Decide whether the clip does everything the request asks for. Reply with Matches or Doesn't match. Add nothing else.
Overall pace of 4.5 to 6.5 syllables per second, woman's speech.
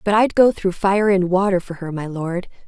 Matches